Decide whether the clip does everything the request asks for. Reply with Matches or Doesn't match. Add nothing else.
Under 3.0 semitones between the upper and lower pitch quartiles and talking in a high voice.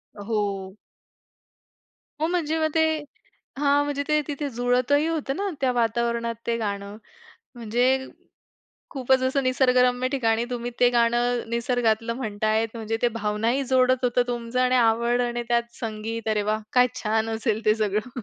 Matches